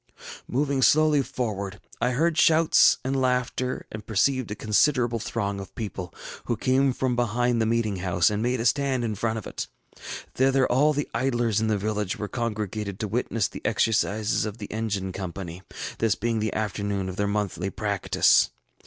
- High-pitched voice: No, low, 110 Hz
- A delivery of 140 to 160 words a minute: No, average, 175 wpm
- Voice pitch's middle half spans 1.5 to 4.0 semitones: Yes, average, 3.7 semitones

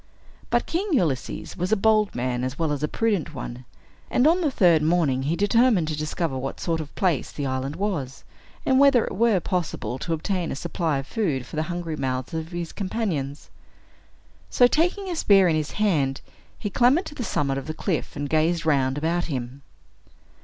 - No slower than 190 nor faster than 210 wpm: Yes, average, 200 wpm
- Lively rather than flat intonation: Yes, wide, 6.7 semitones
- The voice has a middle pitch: Yes, medium, 165 Hz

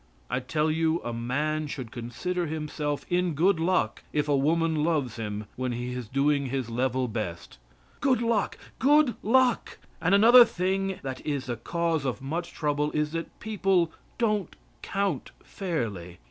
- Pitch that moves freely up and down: Yes, wide, 6.1 semitones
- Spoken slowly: No, average, 160 wpm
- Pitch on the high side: No, medium, 150 Hz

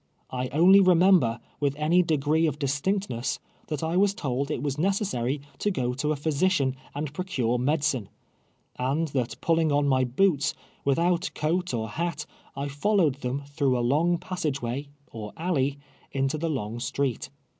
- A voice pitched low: No, medium, 145 Hz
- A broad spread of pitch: No, average, 4.3 semitones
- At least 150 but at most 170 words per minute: Yes, average, 160 wpm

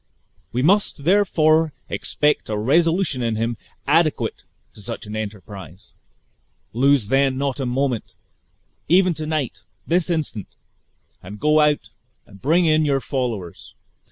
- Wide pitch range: Yes, wide, 5.7 semitones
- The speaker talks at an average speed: No, slow, 130 wpm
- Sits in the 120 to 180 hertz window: Yes, medium, 140 Hz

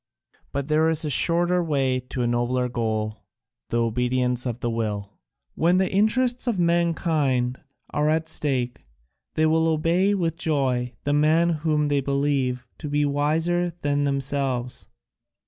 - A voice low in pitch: No, medium, 145 Hz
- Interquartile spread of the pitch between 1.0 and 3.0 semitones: No, average, 4.5 semitones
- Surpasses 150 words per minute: No, average, 145 wpm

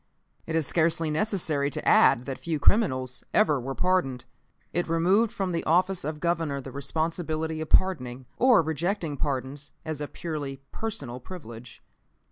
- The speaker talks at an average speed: Yes, average, 150 wpm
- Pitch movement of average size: Yes, average, 4.3 semitones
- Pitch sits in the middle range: Yes, medium, 155 Hz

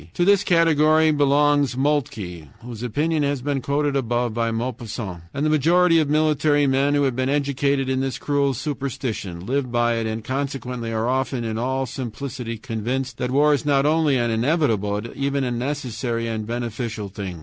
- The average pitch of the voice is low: Yes, low, 130 Hz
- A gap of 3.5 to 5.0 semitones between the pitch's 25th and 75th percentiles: Yes, average, 3.8 semitones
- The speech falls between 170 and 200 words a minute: Yes, average, 180 wpm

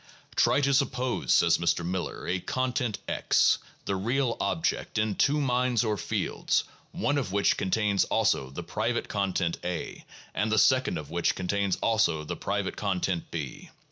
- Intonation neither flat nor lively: No, wide, 5.9 semitones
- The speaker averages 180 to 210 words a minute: No, average, 160 wpm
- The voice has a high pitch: No, low, 105 Hz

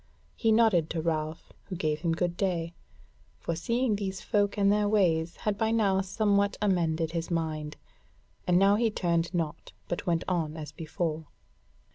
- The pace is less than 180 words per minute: Yes, average, 165 wpm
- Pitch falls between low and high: Yes, medium, 175 Hz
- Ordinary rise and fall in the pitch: Yes, average, 3.8 semitones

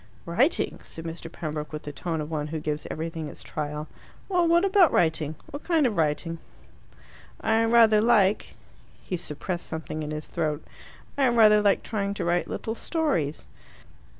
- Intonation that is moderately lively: No, wide, 6.6 semitones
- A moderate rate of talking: Yes, average, 165 wpm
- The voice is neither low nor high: Yes, medium, 170 Hz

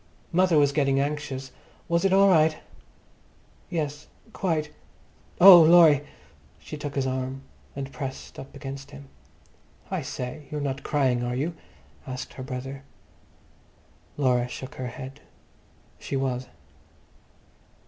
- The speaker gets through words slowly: Yes, slow, 125 wpm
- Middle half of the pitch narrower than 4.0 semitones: Yes, average, 2.8 semitones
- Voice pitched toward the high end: No, medium, 140 Hz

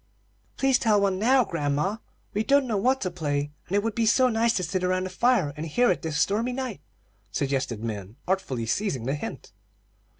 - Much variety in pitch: Yes, wide, 7.7 semitones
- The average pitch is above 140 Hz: Yes, high, 190 Hz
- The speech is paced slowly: No, average, 200 wpm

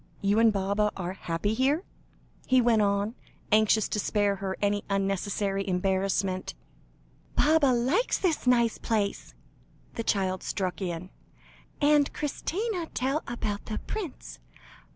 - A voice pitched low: No, high, 210 Hz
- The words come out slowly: Yes, slow, 125 wpm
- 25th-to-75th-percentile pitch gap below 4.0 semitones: No, average, 4.5 semitones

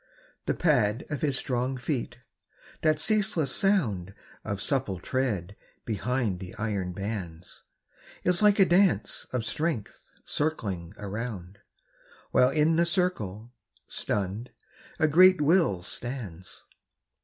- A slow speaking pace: Yes, slow, 115 wpm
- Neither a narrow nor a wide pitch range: No, wide, 7.9 semitones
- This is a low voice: Yes, low, 125 Hz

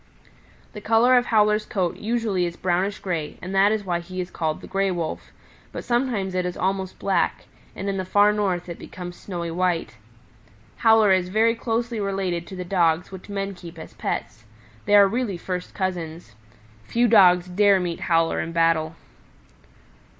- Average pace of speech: Yes, average, 175 wpm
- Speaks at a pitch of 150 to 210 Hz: Yes, medium, 185 Hz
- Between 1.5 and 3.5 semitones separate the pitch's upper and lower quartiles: Yes, average, 2.9 semitones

